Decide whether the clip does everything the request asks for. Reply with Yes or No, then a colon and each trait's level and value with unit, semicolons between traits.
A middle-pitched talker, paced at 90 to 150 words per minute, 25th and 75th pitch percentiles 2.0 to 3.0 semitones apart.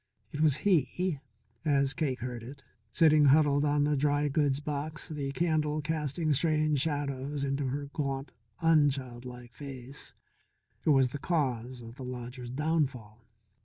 Yes: medium, 145 Hz; average, 145 wpm; average, 2.7 semitones